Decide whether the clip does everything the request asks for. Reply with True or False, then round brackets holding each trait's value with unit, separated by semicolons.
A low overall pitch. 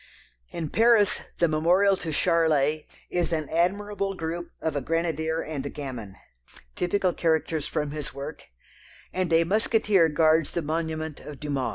False (160 Hz)